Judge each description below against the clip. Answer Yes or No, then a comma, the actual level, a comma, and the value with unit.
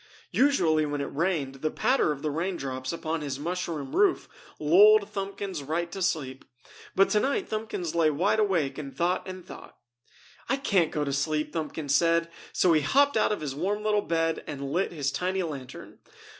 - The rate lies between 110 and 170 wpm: No, average, 180 wpm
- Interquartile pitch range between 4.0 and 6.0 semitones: Yes, average, 4.8 semitones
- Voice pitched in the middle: Yes, medium, 165 Hz